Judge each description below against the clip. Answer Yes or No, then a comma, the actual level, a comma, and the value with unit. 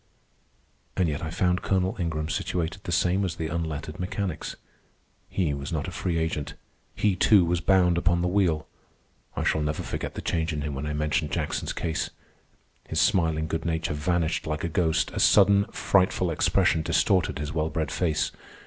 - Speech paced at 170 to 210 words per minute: Yes, average, 180 wpm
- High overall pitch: No, very low, 80 Hz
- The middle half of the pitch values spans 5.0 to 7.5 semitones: No, narrow, 2.6 semitones